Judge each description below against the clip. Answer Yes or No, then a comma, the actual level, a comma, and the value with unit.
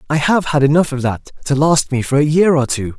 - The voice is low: No, medium, 145 Hz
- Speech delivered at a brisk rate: Yes, fast, 280 wpm